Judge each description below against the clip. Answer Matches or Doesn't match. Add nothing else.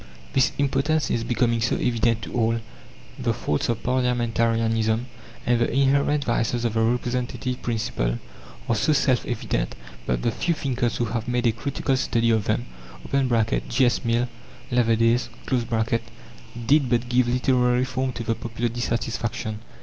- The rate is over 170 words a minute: Doesn't match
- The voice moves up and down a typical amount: Doesn't match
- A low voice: Matches